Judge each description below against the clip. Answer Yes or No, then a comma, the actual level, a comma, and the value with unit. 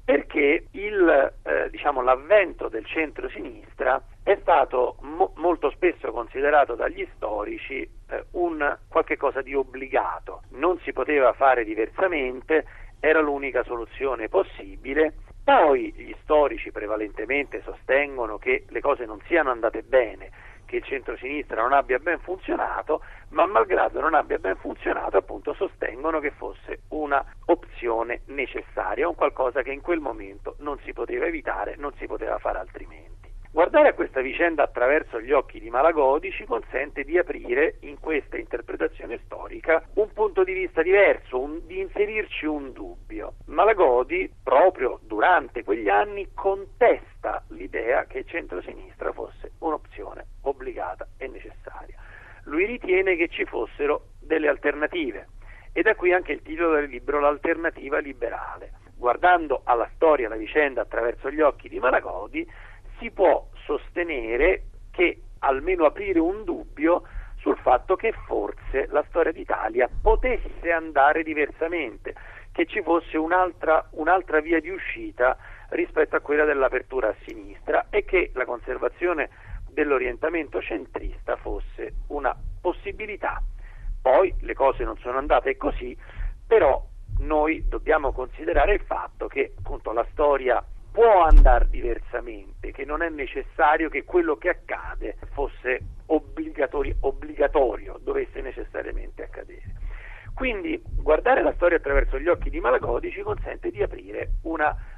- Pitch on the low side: No, very high, 330 Hz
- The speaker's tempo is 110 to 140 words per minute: Yes, average, 135 wpm